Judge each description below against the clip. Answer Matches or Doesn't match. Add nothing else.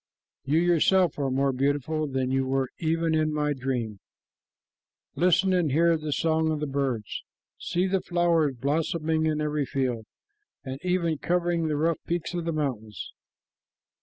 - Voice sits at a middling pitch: Matches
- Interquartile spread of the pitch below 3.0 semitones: Doesn't match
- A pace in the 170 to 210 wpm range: Doesn't match